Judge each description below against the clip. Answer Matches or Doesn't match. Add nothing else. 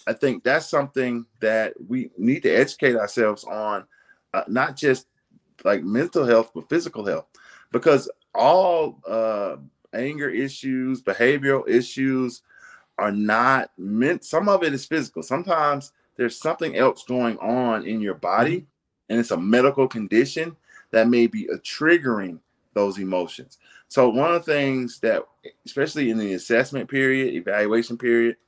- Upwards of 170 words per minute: Doesn't match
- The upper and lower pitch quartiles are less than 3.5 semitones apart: Doesn't match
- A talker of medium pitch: Doesn't match